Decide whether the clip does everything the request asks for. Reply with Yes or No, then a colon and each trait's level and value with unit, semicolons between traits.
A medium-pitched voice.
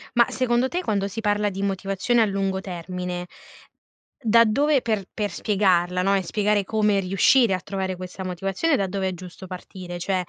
No: high, 195 Hz